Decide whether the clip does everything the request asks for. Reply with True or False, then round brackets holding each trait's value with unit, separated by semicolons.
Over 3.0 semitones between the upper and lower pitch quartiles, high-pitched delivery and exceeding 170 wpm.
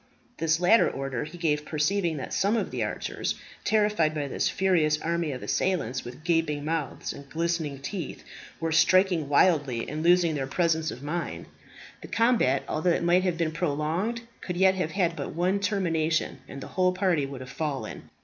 False (3.5 semitones; 165 Hz; 180 wpm)